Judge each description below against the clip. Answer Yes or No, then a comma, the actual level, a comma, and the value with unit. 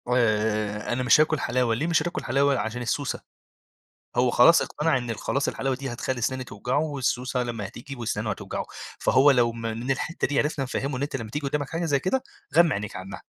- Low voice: Yes, low, 130 Hz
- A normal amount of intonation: Yes, average, 3.6 semitones